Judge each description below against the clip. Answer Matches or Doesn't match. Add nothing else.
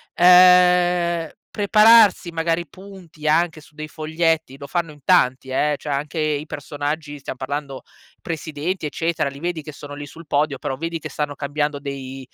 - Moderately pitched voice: Matches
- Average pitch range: Matches